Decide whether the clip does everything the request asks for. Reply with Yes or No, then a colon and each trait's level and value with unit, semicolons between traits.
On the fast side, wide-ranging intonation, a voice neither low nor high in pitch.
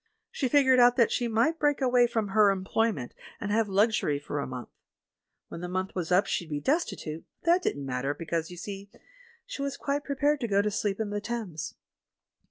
No: fast, 210 wpm; wide, 6.2 semitones; high, 210 Hz